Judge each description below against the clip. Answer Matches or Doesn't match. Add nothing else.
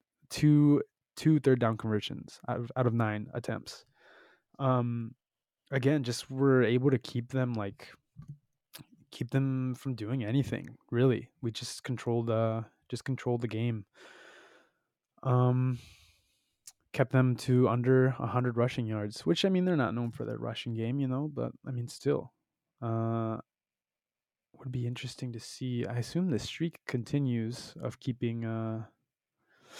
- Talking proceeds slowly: Doesn't match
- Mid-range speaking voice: Doesn't match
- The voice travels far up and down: Doesn't match